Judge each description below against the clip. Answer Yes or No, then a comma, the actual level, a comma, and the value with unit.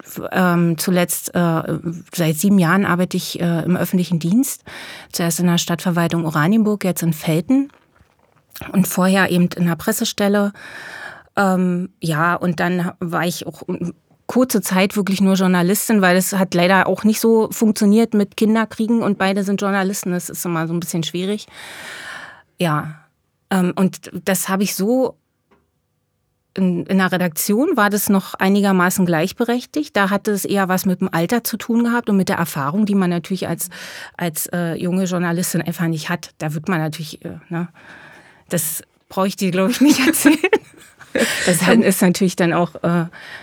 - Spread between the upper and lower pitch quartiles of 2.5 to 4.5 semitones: Yes, average, 2.8 semitones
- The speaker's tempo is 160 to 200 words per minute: Yes, average, 170 wpm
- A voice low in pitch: No, medium, 185 Hz